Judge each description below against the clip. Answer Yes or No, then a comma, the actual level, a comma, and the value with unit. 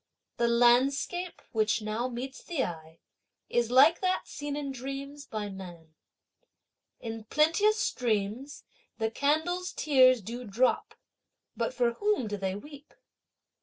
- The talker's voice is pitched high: Yes, very high, 255 Hz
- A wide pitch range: No, average, 5.0 semitones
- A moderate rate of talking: No, slow, 130 wpm